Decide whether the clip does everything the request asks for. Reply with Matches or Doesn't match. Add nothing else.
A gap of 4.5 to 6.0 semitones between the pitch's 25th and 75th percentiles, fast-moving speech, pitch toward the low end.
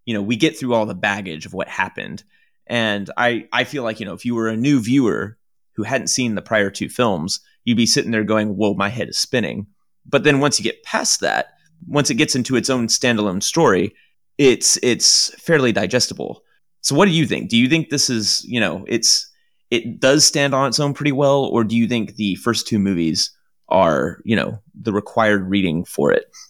Matches